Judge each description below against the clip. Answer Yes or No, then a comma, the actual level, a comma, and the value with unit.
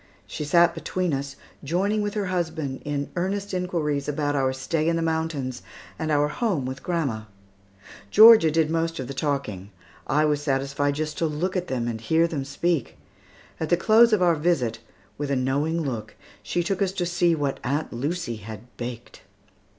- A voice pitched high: No, medium, 155 Hz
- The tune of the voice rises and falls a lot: No, average, 4.1 semitones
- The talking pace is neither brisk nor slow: Yes, average, 180 wpm